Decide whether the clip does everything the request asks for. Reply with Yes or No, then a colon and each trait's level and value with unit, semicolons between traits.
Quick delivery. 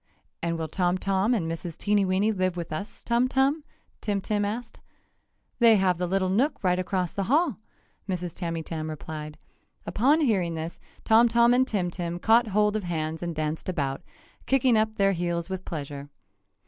No: average, 175 wpm